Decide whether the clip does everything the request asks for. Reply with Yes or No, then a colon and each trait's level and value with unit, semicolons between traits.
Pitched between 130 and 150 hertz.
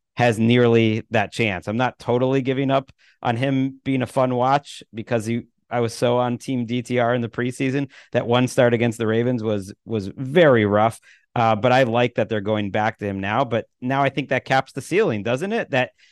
No: low, 120 Hz